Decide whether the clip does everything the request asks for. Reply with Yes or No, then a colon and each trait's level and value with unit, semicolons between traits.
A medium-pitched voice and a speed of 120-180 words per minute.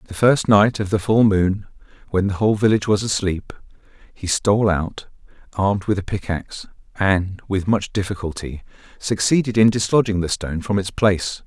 No: low, 100 Hz; average, 165 wpm